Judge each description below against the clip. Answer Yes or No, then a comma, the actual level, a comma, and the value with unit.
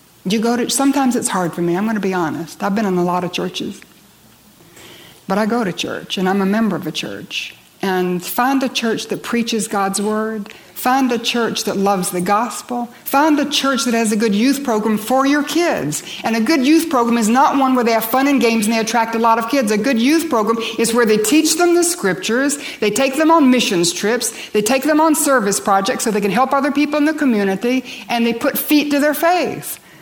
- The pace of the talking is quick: Yes, fast, 240 wpm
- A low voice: No, high, 235 Hz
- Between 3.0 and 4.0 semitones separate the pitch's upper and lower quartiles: No, average, 4.5 semitones